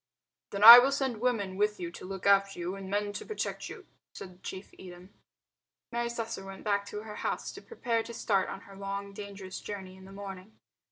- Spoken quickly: Yes, fast, 210 wpm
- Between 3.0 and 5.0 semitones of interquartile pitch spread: No, narrow, 2.4 semitones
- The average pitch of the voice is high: Yes, high, 200 Hz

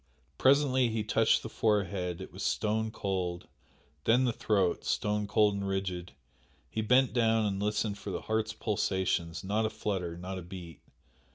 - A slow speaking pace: No, average, 165 wpm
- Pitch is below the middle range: Yes, low, 105 Hz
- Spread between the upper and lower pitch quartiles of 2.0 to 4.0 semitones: Yes, average, 2.8 semitones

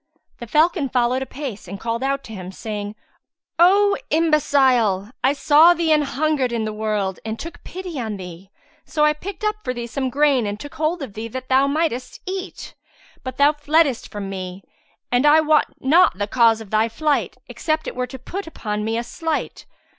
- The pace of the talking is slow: No, average, 195 wpm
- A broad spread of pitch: Yes, wide, 5.9 semitones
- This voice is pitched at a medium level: No, very high, 260 Hz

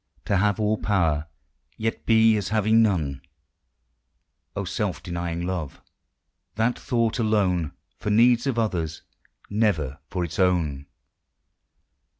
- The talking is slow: Yes, slow, 120 wpm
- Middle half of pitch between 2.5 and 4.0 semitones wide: No, average, 4.7 semitones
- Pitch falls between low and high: No, low, 100 Hz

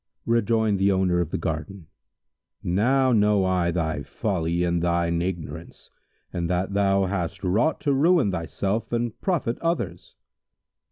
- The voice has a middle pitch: No, very low, 95 Hz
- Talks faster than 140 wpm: No, slow, 135 wpm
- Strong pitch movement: No, average, 4.7 semitones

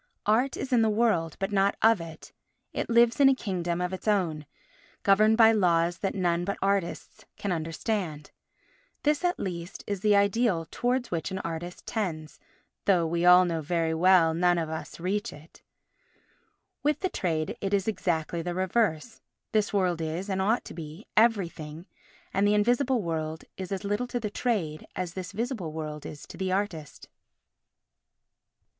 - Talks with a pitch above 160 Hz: Yes, medium, 185 Hz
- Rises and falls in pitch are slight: No, average, 4.4 semitones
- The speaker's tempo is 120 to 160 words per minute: No, average, 175 wpm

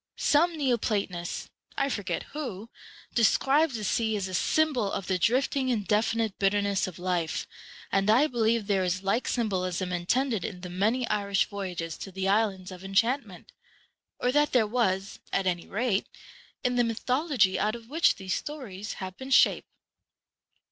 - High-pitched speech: Yes, high, 210 Hz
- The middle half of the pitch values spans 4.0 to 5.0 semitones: Yes, average, 4.7 semitones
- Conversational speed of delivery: Yes, average, 160 wpm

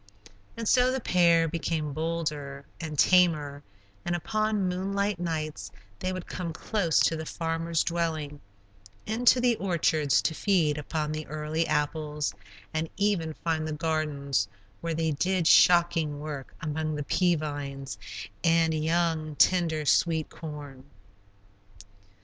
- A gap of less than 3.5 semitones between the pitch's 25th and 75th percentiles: Yes, narrow, 2.5 semitones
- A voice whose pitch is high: No, medium, 160 Hz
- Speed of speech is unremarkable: No, slow, 130 wpm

